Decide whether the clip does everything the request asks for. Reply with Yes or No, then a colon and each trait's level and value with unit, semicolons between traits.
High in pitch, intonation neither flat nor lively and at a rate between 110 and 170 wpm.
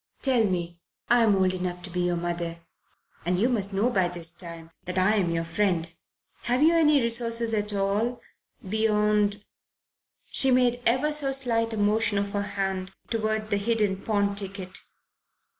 Yes: high, 205 Hz; average, 3.8 semitones; average, 165 wpm